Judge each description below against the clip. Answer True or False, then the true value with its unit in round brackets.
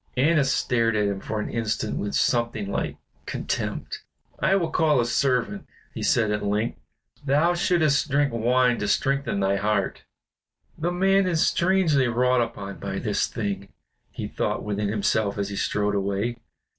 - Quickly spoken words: False (160 wpm)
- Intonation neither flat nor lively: False (5.7 semitones)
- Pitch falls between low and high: False (120 Hz)